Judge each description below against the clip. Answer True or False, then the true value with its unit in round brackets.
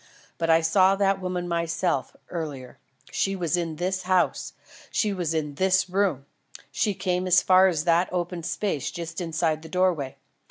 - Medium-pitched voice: True (175 Hz)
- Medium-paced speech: True (165 wpm)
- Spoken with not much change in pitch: True (2.3 semitones)